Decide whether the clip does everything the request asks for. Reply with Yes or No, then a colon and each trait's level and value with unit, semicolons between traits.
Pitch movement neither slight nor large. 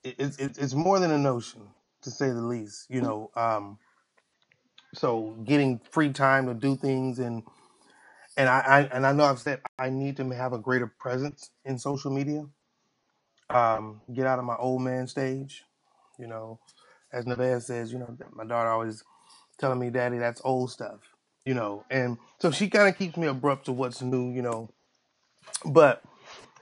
No: narrow, 2.3 semitones